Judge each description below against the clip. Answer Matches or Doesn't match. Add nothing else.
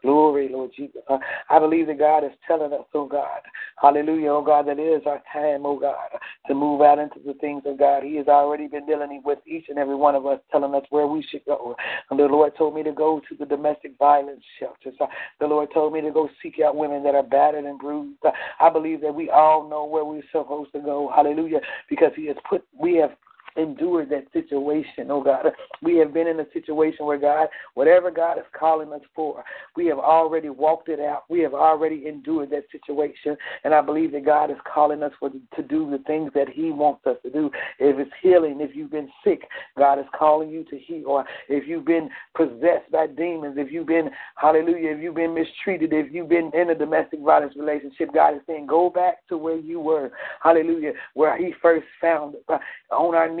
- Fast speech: Matches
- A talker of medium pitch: Matches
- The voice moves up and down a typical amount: Doesn't match